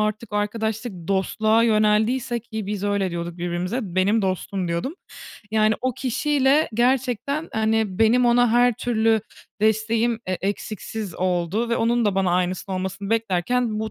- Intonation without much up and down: No, average, 3.6 semitones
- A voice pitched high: Yes, high, 220 Hz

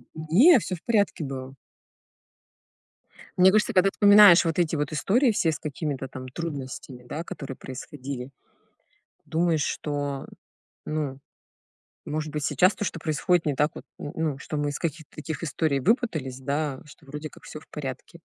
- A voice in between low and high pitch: Yes, medium, 155 Hz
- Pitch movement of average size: Yes, average, 3.5 semitones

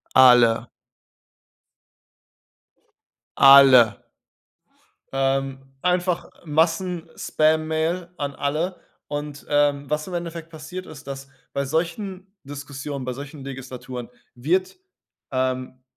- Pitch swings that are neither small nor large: Yes, average, 3.5 semitones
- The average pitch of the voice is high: No, medium, 145 Hz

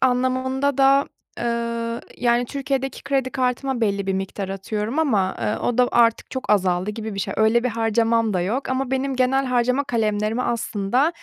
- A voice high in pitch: Yes, high, 235 Hz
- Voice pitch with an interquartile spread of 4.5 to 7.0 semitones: No, average, 3.5 semitones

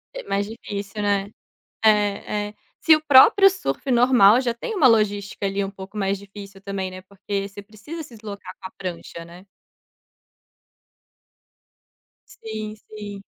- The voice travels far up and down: No, narrow, 2.5 semitones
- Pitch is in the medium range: No, high, 205 Hz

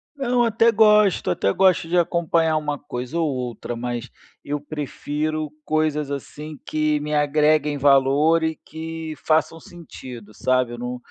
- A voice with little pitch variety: No, average, 3.0 semitones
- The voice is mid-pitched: Yes, medium, 150 Hz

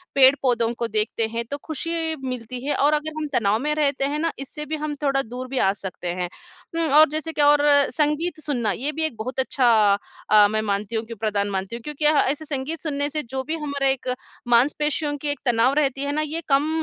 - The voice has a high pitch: Yes, very high, 275 Hz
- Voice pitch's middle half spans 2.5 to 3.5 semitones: No, average, 4.4 semitones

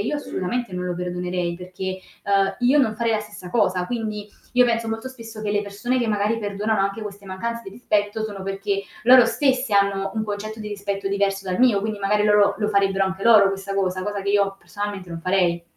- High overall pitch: Yes, high, 205 Hz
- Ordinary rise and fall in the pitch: No, narrow, 2.2 semitones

